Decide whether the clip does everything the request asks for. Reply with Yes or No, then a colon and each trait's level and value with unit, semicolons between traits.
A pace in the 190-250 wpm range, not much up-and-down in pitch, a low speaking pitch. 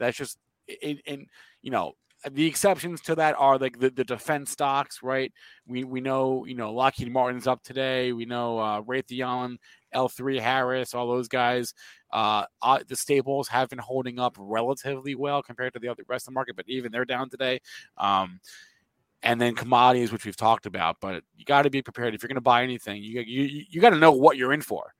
Yes: fast, 205 wpm; narrow, 1.9 semitones; low, 130 Hz